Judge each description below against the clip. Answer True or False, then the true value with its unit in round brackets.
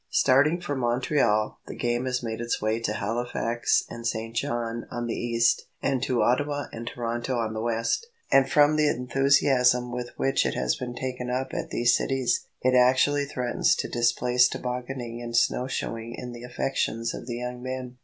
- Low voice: True (125 Hz)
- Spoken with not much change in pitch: True (1.8 semitones)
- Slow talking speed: False (185 wpm)